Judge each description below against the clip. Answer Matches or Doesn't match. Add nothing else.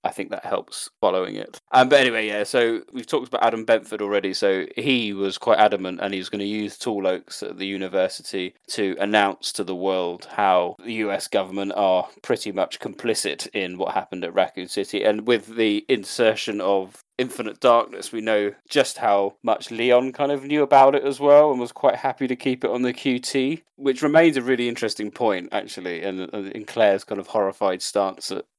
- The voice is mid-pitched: Doesn't match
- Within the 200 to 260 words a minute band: Matches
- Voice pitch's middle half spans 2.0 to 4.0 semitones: Doesn't match